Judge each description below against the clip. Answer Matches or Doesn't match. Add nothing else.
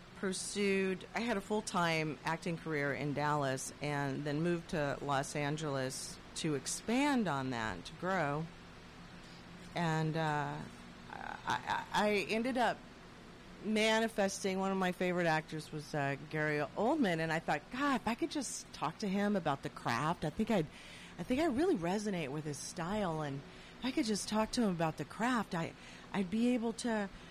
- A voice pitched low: Doesn't match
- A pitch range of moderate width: Doesn't match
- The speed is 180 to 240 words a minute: Doesn't match